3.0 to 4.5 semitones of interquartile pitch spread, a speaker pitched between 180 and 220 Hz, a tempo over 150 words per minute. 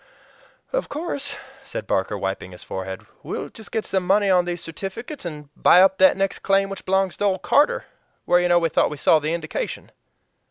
Yes: average, 3.9 semitones; medium, 185 Hz; average, 200 wpm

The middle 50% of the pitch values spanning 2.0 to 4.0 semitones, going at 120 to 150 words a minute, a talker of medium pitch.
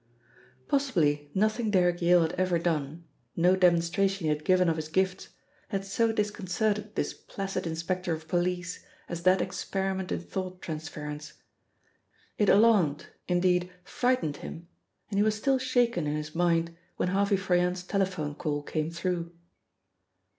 Yes: average, 3.0 semitones; average, 145 wpm; medium, 180 Hz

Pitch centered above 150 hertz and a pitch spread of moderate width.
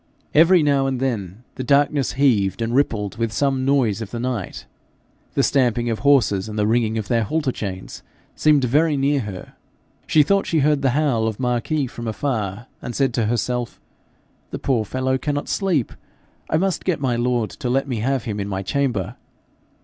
No: low, 125 Hz; average, 4.1 semitones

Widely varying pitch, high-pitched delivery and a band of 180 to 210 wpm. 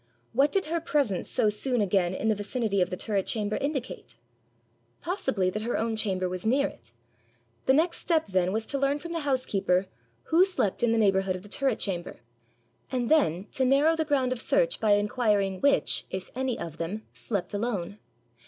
Yes: wide, 6.1 semitones; high, 220 Hz; average, 190 wpm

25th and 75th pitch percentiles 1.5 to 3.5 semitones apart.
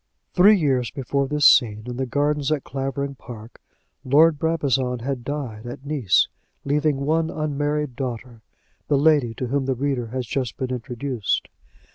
Yes: average, 3.0 semitones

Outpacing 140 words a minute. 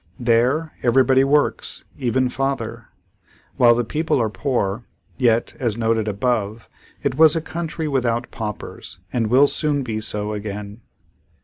No: slow, 135 wpm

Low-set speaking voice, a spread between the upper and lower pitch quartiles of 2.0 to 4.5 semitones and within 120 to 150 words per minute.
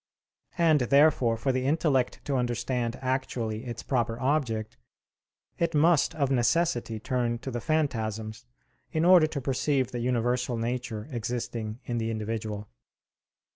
Yes: low, 125 Hz; average, 3.5 semitones; slow, 135 wpm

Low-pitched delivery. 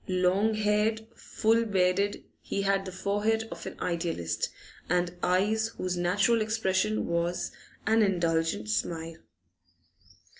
No: high, 190 Hz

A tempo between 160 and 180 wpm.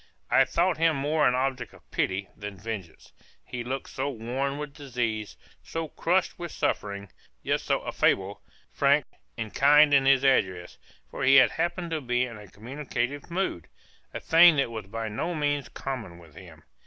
Yes: average, 170 wpm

